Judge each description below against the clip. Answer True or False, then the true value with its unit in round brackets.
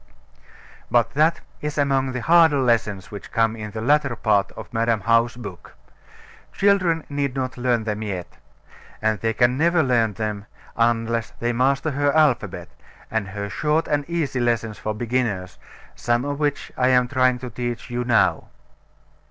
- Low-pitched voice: True (120 Hz)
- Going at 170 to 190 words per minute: False (160 wpm)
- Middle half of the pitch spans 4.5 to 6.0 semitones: False (4.1 semitones)